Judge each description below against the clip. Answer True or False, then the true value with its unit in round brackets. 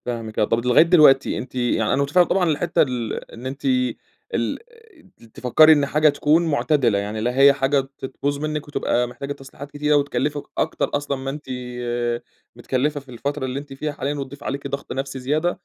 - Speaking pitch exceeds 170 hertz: False (140 Hz)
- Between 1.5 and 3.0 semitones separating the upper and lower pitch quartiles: True (2.7 semitones)